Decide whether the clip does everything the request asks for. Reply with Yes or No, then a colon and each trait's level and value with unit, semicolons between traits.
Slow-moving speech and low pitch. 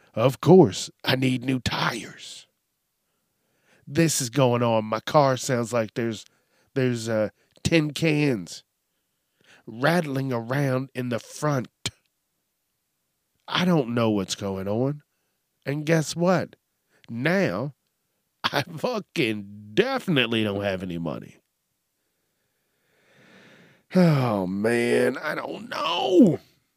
Yes: slow, 105 wpm; low, 125 Hz